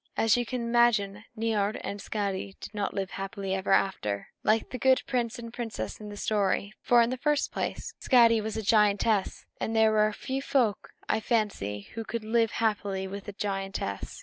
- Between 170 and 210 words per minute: Yes, average, 195 wpm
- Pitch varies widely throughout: No, average, 2.7 semitones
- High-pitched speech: Yes, high, 215 Hz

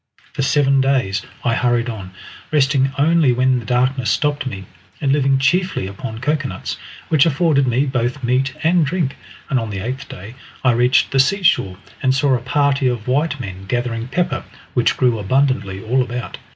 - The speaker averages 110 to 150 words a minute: No, average, 175 wpm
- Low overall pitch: Yes, low, 130 Hz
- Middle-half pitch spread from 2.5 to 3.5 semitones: Yes, average, 3.0 semitones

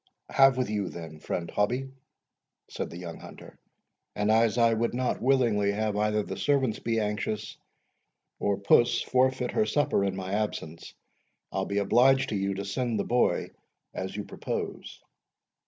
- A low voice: Yes, low, 105 Hz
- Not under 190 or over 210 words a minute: No, average, 160 wpm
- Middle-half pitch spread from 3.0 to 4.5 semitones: Yes, average, 3.8 semitones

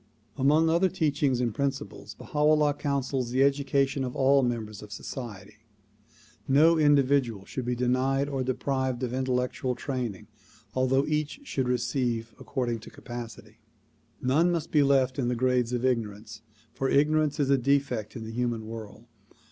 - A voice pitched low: Yes, low, 130 Hz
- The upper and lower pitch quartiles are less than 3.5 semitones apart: Yes, average, 2.7 semitones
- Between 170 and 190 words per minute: No, average, 155 wpm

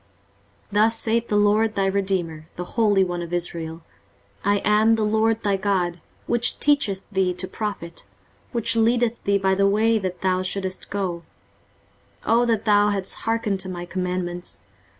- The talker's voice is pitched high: Yes, high, 200 Hz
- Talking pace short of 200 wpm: Yes, average, 170 wpm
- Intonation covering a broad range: No, average, 3.2 semitones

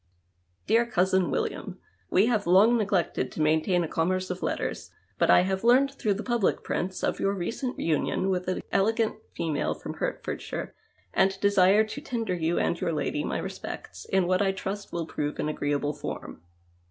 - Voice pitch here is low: No, high, 190 Hz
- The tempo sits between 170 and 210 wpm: Yes, average, 185 wpm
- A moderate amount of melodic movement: Yes, average, 3.7 semitones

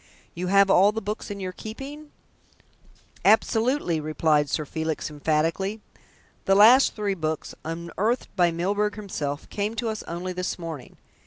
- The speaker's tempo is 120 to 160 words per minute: Yes, average, 150 wpm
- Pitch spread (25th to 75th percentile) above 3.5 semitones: Yes, average, 4.7 semitones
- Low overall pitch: No, high, 190 Hz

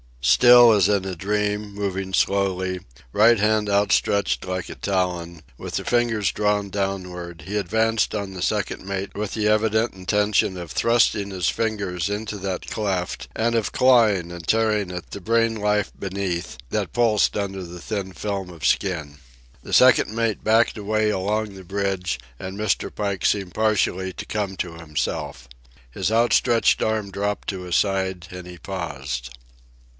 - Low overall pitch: Yes, low, 100 Hz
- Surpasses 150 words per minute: Yes, average, 160 wpm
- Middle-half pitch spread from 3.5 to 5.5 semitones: No, average, 2.7 semitones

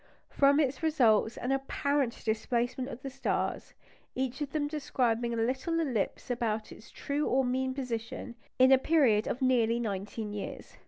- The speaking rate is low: No, average, 160 wpm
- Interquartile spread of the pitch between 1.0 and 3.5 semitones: Yes, average, 3.1 semitones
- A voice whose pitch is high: Yes, very high, 255 Hz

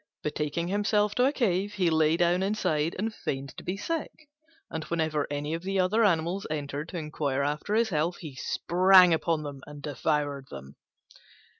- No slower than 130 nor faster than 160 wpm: No, average, 175 wpm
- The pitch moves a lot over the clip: No, average, 4.6 semitones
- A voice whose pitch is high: No, medium, 165 Hz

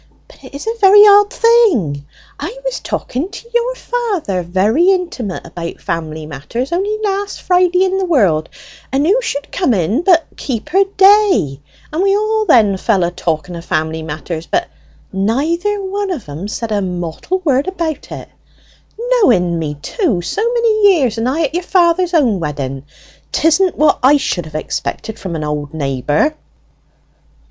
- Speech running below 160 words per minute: No, average, 165 wpm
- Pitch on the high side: Yes, very high, 280 Hz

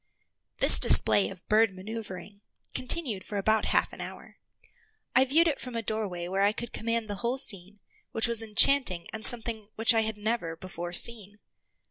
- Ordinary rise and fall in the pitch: Yes, average, 3.2 semitones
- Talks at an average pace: Yes, average, 175 wpm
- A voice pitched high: Yes, high, 215 Hz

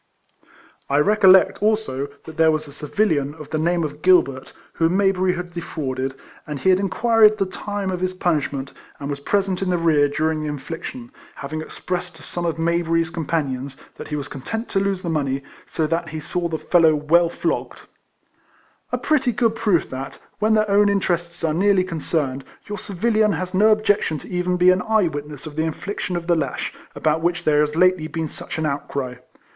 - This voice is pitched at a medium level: Yes, medium, 170 Hz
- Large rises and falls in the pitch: No, average, 4.0 semitones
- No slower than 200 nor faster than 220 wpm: Yes, fast, 205 wpm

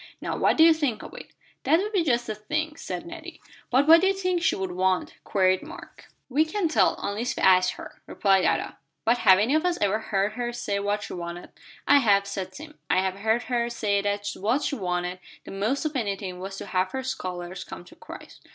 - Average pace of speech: No, fast, 230 wpm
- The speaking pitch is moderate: No, high, 215 Hz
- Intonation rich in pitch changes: Yes, wide, 7.3 semitones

